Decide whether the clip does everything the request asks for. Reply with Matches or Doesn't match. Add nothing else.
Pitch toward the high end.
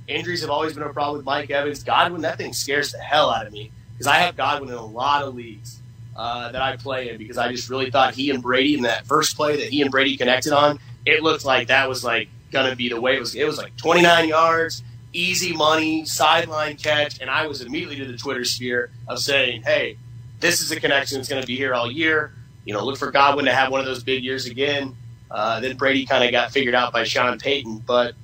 Doesn't match